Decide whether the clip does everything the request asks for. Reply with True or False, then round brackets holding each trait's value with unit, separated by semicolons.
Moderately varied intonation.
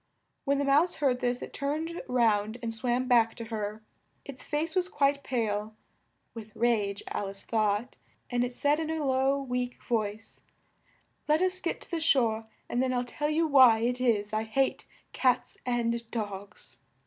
True (4.0 semitones)